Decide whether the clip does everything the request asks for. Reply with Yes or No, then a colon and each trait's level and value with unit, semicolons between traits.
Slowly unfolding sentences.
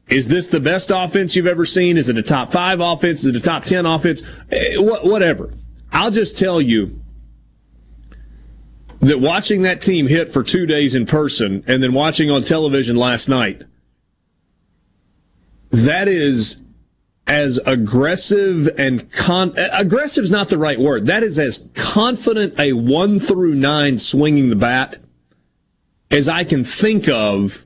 No: average, 150 wpm